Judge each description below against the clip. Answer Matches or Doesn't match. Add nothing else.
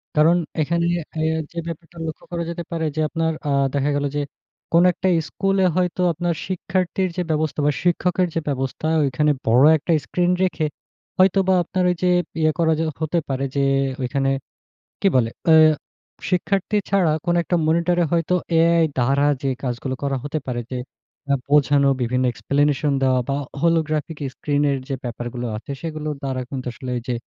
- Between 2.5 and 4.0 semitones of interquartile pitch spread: Matches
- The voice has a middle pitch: Matches